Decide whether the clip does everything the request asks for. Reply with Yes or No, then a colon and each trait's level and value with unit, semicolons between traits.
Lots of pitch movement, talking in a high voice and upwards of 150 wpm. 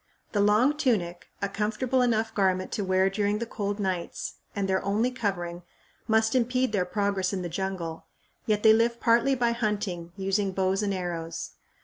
No: average, 3.1 semitones; high, 205 Hz; average, 170 wpm